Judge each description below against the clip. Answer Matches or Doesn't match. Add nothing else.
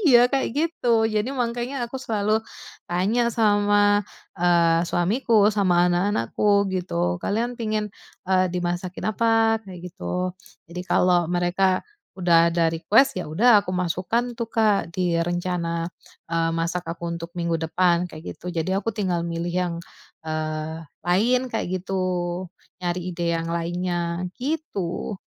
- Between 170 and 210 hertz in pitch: Matches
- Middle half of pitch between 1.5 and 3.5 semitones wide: Doesn't match